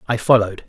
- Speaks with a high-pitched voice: No, low, 110 Hz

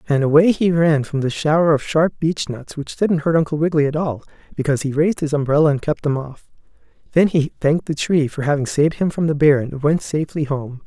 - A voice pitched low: No, medium, 150 Hz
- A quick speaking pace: Yes, fast, 235 wpm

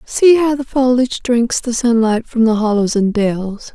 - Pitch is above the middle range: Yes, high, 235 Hz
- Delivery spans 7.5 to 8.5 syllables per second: No, 4.4 syllables/s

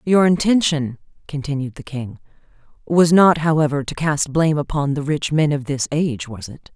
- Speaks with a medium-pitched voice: Yes, medium, 145 Hz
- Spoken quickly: No, average, 180 wpm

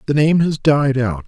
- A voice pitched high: No, medium, 140 Hz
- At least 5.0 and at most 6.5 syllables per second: No, 4.5 syllables/s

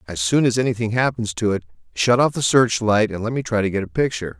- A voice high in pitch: No, low, 115 Hz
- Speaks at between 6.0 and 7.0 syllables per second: Yes, 6.4 syllables/s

